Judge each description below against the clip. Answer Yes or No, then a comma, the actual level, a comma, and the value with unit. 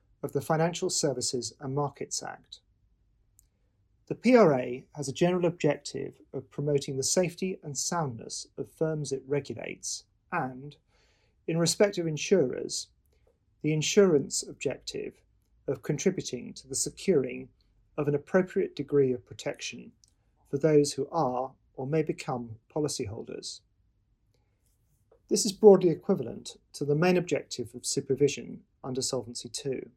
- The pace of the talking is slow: Yes, slow, 125 wpm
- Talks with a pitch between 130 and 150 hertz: Yes, medium, 140 Hz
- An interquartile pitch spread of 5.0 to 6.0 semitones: Yes, wide, 5.5 semitones